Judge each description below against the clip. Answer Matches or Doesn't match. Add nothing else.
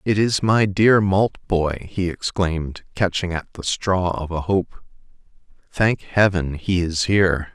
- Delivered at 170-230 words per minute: Doesn't match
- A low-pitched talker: Matches